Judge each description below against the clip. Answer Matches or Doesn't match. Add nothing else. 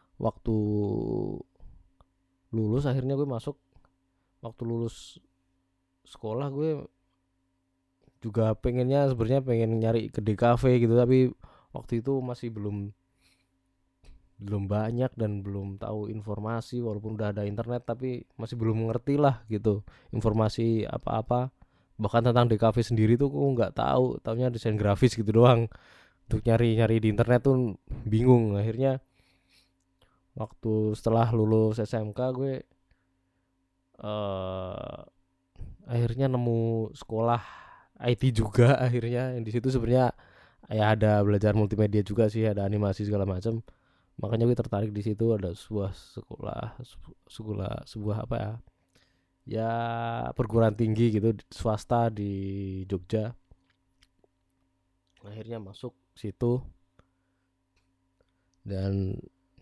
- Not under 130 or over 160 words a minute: Doesn't match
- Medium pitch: Doesn't match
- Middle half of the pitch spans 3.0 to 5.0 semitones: Matches